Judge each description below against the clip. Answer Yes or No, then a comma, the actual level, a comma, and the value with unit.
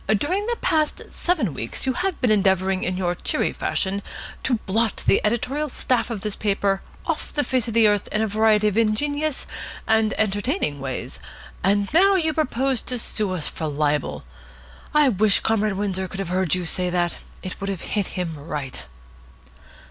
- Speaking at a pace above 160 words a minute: Yes, average, 180 wpm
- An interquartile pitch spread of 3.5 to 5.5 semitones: Yes, average, 5.2 semitones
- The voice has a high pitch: Yes, high, 210 Hz